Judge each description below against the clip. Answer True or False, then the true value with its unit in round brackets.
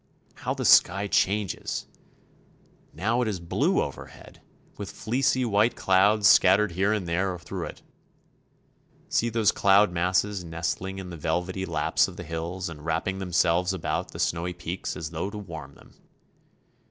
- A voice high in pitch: False (95 Hz)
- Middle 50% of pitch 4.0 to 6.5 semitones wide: False (3.2 semitones)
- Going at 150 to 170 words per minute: True (155 wpm)